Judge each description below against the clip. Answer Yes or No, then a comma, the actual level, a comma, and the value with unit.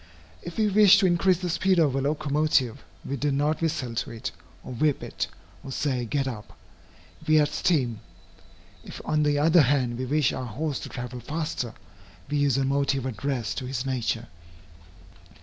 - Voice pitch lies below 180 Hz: Yes, medium, 140 Hz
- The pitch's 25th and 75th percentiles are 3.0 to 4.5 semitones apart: Yes, average, 3.5 semitones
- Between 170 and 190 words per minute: Yes, average, 180 wpm